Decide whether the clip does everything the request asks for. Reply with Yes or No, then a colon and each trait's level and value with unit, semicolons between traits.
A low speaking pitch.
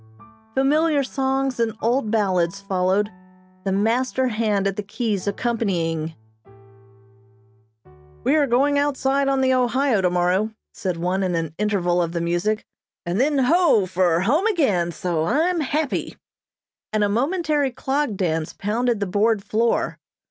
No: high, 215 Hz